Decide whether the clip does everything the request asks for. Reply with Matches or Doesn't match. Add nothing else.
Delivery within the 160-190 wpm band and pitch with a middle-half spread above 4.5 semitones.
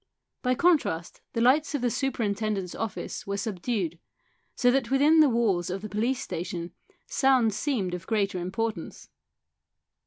Doesn't match